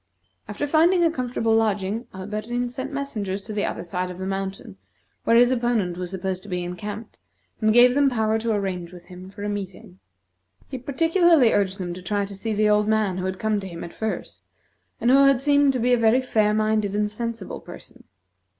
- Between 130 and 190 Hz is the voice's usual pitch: No, high, 215 Hz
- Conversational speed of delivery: No, fast, 210 wpm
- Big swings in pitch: No, average, 4.3 semitones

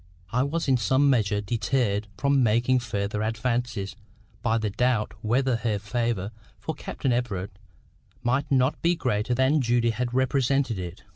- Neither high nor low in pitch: No, low, 120 Hz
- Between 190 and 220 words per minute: No, average, 150 wpm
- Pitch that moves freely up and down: No, average, 3.5 semitones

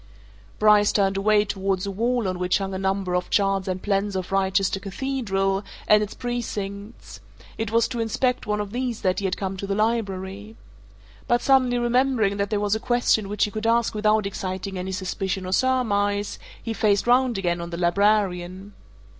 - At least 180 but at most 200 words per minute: Yes, average, 190 wpm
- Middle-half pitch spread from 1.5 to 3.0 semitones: Yes, average, 2.7 semitones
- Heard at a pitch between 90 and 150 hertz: No, high, 200 Hz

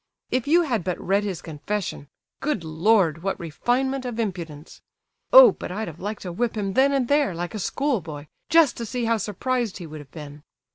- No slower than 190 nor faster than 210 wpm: Yes, average, 195 wpm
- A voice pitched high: Yes, high, 205 Hz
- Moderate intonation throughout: No, wide, 7.0 semitones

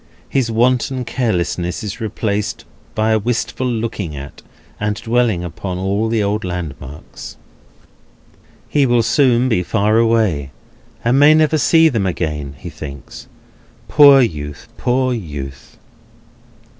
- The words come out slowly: Yes, slow, 125 wpm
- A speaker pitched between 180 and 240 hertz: No, low, 110 Hz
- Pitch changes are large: Yes, wide, 5.8 semitones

